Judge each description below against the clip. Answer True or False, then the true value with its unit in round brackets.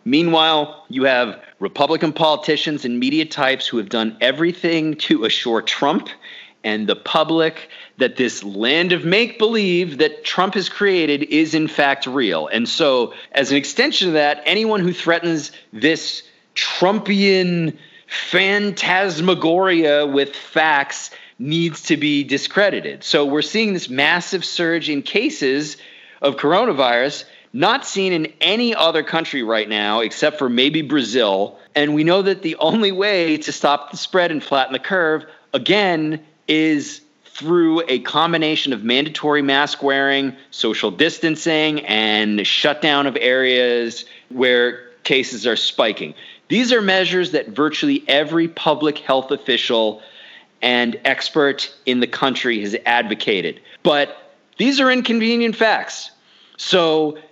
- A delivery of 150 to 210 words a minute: False (135 wpm)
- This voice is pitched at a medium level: True (155 Hz)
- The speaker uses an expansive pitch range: False (4.5 semitones)